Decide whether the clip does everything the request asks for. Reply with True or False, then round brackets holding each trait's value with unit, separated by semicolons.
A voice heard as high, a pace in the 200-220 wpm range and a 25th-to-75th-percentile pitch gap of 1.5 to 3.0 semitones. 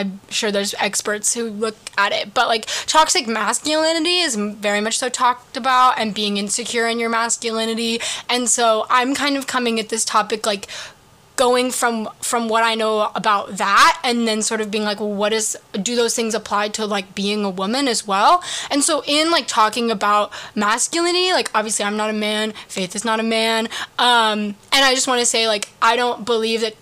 True (225 Hz; 205 wpm; 2.6 semitones)